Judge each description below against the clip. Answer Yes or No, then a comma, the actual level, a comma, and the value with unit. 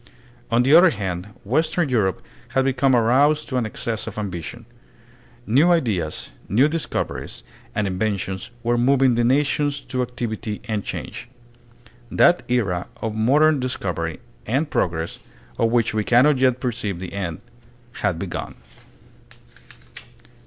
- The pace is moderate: No, slow, 130 wpm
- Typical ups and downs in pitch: Yes, average, 5.0 semitones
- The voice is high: No, low, 120 Hz